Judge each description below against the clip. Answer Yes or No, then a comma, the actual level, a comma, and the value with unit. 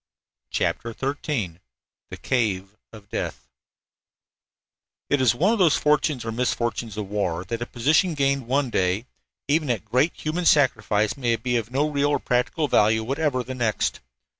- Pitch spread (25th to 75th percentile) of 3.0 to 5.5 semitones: Yes, average, 4.7 semitones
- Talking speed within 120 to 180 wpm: Yes, average, 160 wpm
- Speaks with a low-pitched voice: Yes, low, 125 Hz